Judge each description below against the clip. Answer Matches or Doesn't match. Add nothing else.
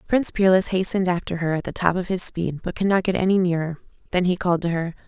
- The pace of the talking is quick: Matches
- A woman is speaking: Matches